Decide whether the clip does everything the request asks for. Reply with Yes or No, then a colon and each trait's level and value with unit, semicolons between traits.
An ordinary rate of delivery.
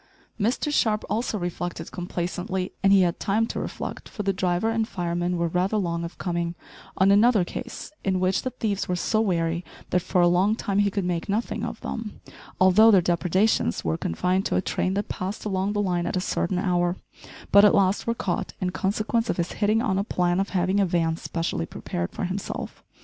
No: fast, 210 wpm